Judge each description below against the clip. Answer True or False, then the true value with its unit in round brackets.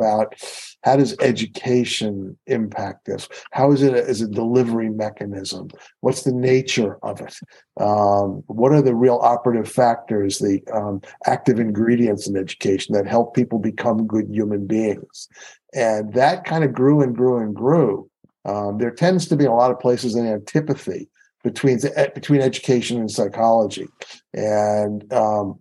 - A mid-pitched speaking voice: False (115 Hz)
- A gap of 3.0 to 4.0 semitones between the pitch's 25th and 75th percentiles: True (3.4 semitones)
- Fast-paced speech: False (155 wpm)